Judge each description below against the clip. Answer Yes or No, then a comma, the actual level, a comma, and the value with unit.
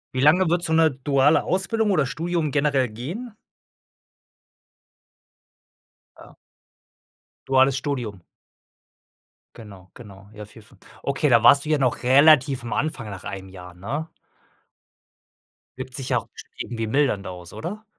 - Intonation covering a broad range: Yes, wide, 6.0 semitones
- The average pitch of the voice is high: No, low, 135 Hz